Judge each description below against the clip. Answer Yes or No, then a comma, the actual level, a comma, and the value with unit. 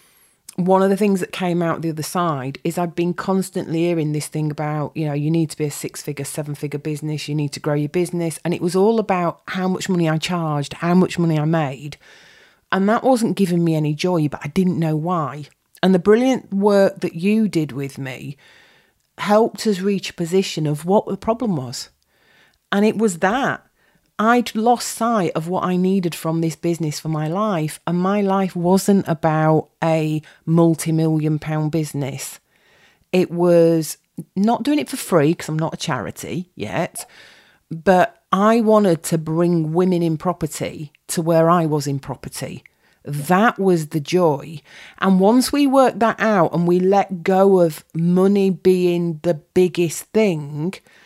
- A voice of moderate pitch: Yes, medium, 170 Hz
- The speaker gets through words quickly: No, average, 185 wpm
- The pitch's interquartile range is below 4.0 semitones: Yes, average, 3.6 semitones